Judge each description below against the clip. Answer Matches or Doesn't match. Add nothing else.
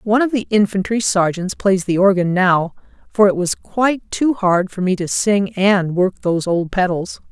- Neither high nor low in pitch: Doesn't match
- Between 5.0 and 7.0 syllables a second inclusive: Doesn't match